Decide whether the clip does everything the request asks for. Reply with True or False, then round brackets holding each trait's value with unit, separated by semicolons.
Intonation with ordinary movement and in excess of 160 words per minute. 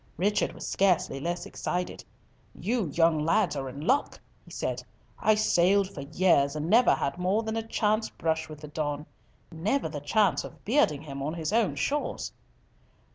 False (5.8 semitones; 175 wpm)